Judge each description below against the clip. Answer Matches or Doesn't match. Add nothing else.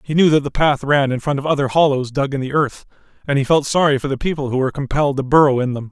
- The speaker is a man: Matches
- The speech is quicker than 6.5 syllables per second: Matches